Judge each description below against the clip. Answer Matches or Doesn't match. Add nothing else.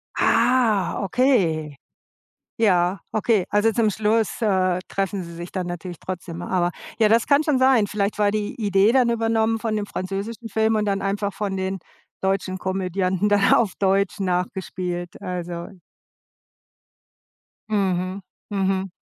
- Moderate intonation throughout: Matches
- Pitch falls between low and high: Doesn't match